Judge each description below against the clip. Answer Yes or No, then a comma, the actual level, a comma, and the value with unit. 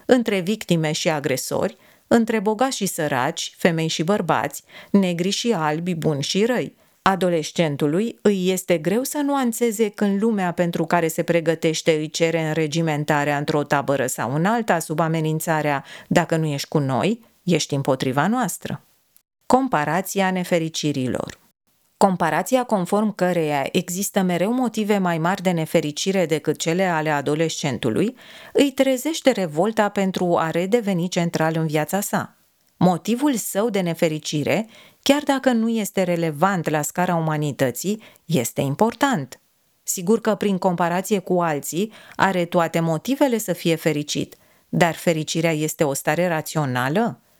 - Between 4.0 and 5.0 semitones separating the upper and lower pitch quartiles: Yes, average, 4.7 semitones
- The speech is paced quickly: No, average, 135 wpm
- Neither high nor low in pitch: Yes, medium, 175 Hz